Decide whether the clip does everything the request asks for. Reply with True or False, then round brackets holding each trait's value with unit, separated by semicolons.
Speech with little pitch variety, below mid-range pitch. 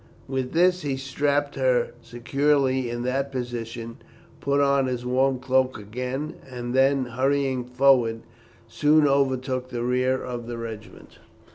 True (2.1 semitones; 130 Hz)